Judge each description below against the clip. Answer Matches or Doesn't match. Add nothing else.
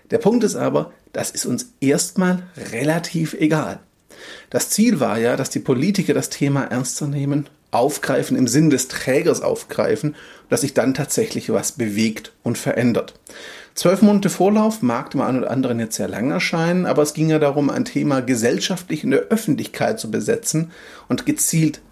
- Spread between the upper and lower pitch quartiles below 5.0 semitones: Matches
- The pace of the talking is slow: Doesn't match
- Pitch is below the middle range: Doesn't match